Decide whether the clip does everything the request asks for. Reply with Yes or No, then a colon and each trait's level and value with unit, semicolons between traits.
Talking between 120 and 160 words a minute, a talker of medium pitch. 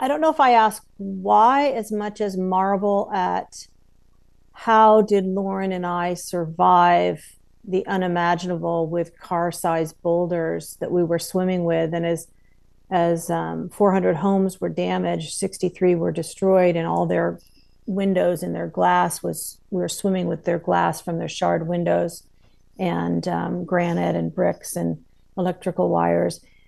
Yes: average, 145 wpm; medium, 170 Hz